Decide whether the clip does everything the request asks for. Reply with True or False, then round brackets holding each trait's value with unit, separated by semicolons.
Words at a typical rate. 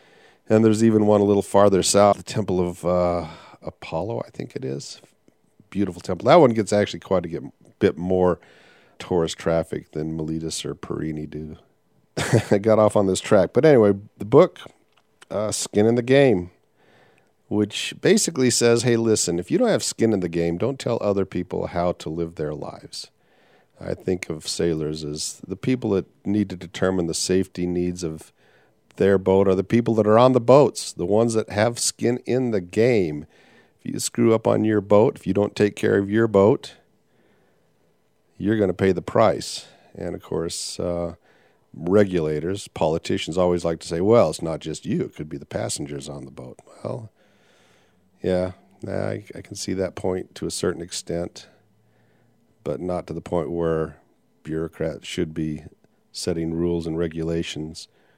True (175 wpm)